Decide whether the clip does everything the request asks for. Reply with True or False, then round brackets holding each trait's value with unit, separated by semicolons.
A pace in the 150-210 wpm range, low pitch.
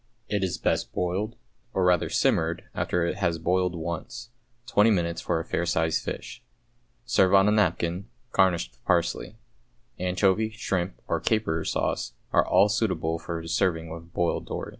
True (160 wpm; 90 Hz)